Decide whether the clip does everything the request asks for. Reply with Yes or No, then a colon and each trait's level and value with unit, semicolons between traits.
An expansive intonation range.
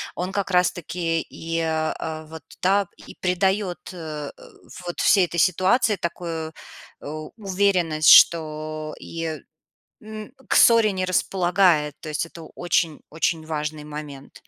No: average, 3.0 semitones